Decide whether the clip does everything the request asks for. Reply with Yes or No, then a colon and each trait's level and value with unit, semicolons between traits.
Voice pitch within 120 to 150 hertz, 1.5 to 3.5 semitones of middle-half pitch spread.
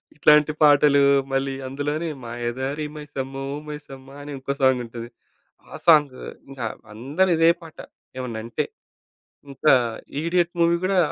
Yes: medium, 140 Hz; narrow, 2.6 semitones